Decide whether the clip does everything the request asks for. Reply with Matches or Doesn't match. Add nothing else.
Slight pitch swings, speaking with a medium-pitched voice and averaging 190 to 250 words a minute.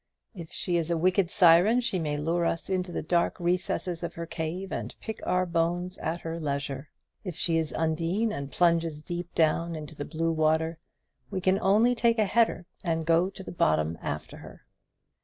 Matches